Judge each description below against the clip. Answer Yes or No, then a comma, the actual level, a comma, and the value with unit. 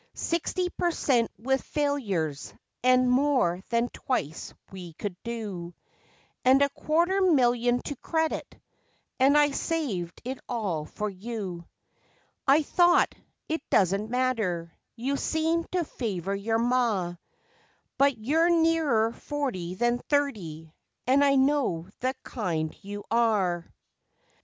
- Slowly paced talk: Yes, slow, 120 wpm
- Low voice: No, high, 245 Hz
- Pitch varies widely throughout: Yes, wide, 6.7 semitones